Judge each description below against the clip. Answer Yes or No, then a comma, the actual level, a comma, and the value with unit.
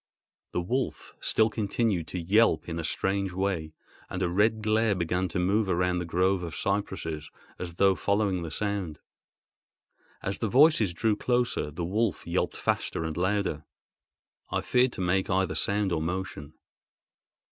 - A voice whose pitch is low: Yes, very low, 95 Hz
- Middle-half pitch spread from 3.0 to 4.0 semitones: Yes, average, 3.3 semitones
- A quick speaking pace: No, average, 160 wpm